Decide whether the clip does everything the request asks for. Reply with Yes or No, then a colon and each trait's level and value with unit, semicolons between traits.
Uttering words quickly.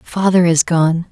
No: average, 160 wpm